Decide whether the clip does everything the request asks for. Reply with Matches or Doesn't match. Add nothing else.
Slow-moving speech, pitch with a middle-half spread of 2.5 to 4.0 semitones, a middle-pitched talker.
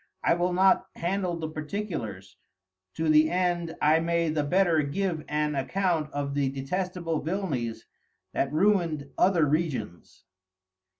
Matches